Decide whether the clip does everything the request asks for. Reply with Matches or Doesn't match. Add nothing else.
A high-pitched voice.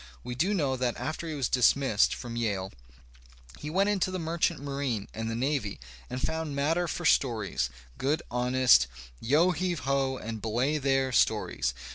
Doesn't match